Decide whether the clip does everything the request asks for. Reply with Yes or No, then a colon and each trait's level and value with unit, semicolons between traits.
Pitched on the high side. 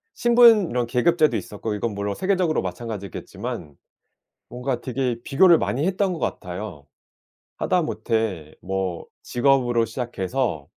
No: low, 120 Hz